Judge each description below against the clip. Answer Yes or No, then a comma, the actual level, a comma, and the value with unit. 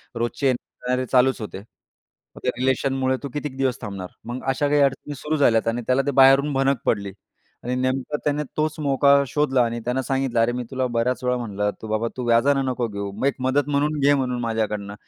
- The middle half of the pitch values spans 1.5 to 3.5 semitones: Yes, average, 2.8 semitones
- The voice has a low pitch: Yes, low, 130 Hz